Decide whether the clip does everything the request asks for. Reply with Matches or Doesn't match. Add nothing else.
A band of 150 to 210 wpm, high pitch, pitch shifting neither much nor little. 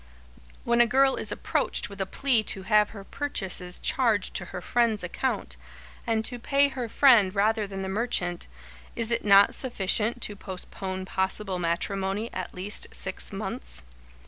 Matches